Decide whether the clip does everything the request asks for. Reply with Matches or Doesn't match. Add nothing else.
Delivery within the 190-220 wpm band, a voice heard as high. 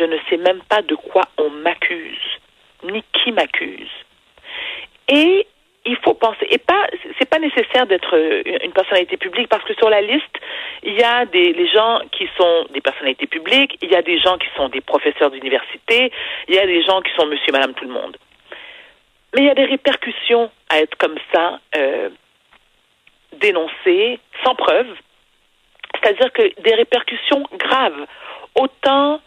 Doesn't match